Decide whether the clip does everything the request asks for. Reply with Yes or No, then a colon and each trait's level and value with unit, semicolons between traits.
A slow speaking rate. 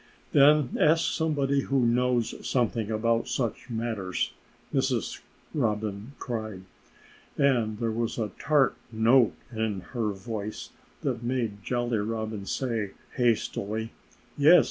Yes: slow, 115 wpm